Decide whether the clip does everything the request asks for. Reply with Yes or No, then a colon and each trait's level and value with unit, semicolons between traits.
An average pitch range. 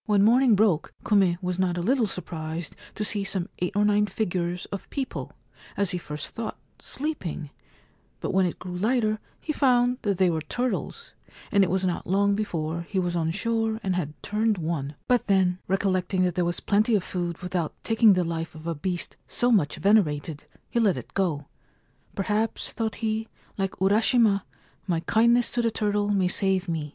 Yes: average, 3.8 semitones